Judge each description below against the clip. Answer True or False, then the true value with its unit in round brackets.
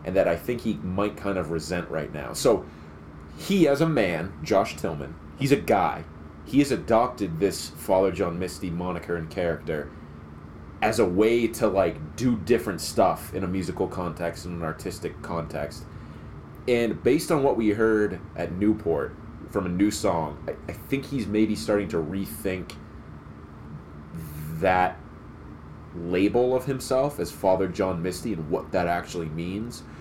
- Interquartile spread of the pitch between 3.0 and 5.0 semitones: False (5.4 semitones)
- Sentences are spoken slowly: False (160 wpm)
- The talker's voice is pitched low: True (90 Hz)